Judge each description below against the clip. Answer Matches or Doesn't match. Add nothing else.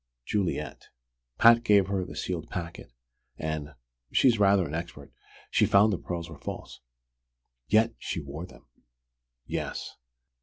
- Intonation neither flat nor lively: Matches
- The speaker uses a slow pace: Matches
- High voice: Doesn't match